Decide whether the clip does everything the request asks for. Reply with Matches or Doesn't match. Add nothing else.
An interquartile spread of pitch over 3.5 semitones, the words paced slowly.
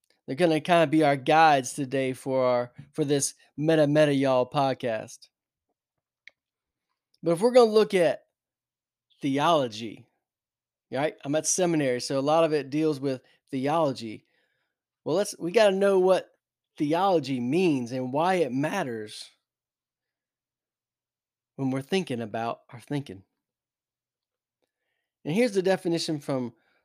Matches